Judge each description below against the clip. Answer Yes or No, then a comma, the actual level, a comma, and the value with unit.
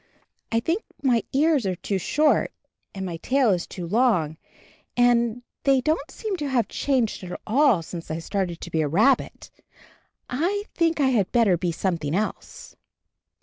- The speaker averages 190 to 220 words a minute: No, average, 170 wpm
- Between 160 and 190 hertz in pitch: No, high, 230 Hz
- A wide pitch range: Yes, wide, 7.3 semitones